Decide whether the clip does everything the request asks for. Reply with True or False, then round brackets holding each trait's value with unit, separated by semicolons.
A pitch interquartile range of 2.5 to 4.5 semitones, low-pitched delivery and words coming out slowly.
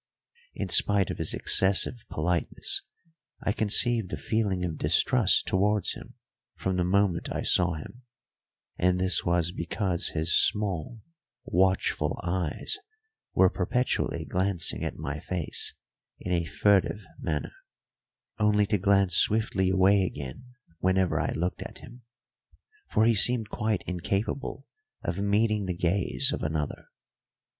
True (2.9 semitones; 95 Hz; 130 wpm)